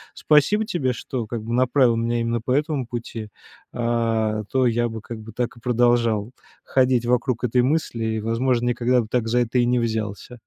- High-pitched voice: No, low, 120 Hz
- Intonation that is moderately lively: No, narrow, 1.7 semitones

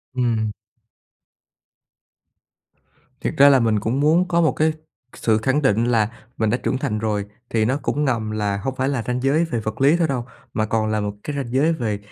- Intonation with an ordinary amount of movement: Yes, average, 4.5 semitones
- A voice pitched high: No, low, 120 Hz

